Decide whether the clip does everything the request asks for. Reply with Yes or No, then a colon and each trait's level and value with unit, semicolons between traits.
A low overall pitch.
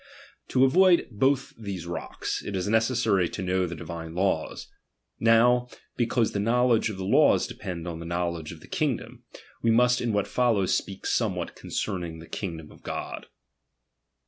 Yes: low, 100 Hz